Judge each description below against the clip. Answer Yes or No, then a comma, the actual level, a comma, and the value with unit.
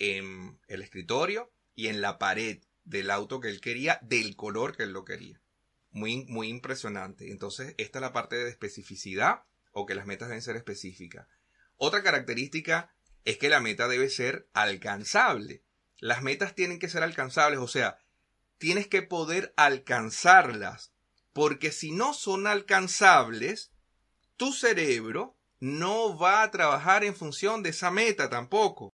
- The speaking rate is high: No, average, 150 wpm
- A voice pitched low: No, medium, 150 Hz